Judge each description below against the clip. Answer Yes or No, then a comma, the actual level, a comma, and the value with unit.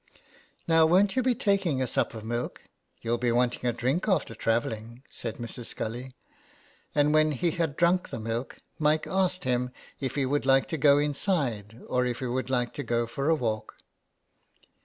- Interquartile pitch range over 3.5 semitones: Yes, average, 4.9 semitones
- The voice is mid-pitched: No, low, 130 Hz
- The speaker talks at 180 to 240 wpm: Yes, average, 190 wpm